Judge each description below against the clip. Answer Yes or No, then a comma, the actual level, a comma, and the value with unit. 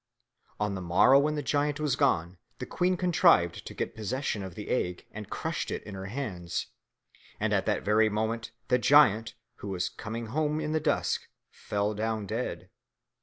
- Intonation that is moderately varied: No, wide, 6.1 semitones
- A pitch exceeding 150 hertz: No, low, 110 Hz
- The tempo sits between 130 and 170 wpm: No, average, 180 wpm